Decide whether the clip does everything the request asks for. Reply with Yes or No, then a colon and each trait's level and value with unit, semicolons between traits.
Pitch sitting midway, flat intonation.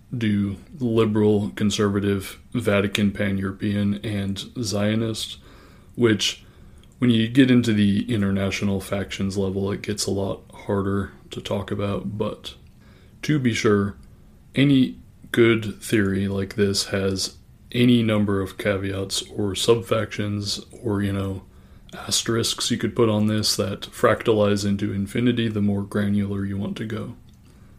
No: low, 100 Hz; narrow, 2.1 semitones